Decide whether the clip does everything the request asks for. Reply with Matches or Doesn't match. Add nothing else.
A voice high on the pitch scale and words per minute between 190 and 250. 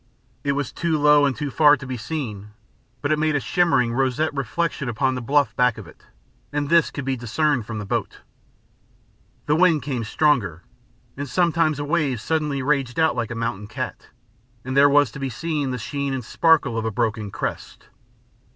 Doesn't match